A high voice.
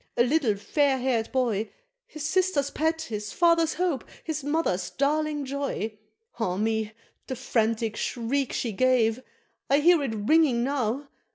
Yes: very high, 265 Hz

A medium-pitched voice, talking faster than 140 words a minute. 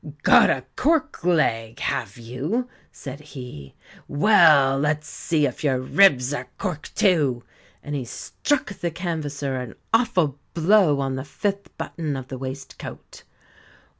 No: medium, 145 Hz; slow, 135 wpm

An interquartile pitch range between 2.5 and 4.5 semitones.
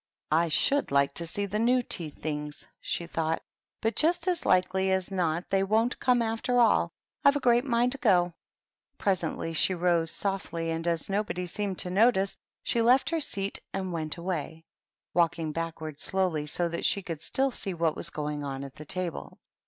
No: average, 5.3 semitones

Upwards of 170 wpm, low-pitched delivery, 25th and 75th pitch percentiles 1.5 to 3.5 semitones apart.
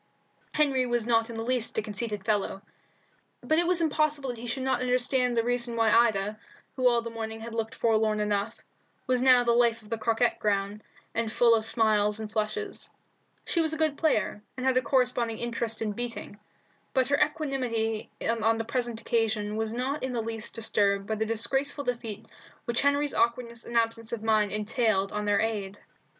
No: average, 190 wpm; high, 230 Hz; narrow, 2.4 semitones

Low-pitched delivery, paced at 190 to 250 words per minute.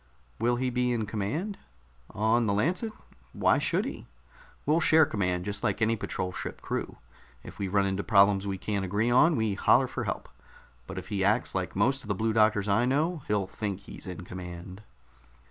Yes: low, 105 Hz; average, 195 wpm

